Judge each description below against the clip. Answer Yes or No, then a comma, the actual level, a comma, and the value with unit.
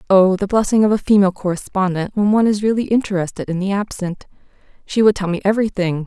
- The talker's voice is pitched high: Yes, high, 195 Hz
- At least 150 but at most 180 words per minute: No, average, 200 wpm